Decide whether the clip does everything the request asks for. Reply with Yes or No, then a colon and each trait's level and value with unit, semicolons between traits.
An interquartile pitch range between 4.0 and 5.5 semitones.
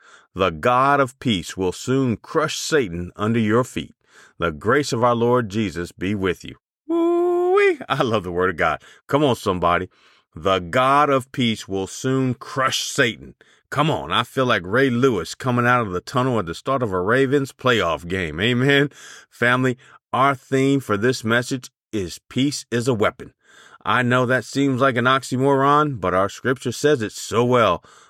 Yes: average, 4.3 semitones